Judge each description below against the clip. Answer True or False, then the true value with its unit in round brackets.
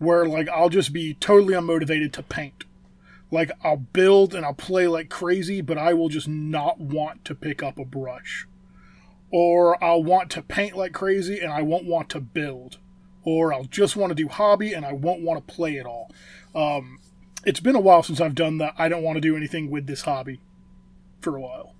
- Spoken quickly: True (210 wpm)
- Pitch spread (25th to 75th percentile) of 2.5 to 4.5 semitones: True (3.5 semitones)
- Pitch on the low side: False (160 Hz)